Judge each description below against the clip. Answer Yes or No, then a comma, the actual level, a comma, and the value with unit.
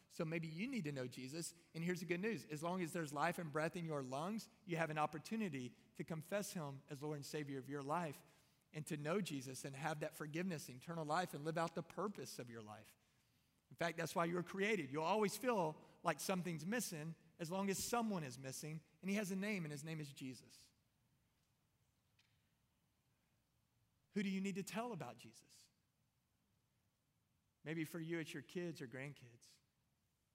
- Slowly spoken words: No, average, 195 wpm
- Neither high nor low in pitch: Yes, medium, 160 Hz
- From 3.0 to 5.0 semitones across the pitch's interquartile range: Yes, average, 4.5 semitones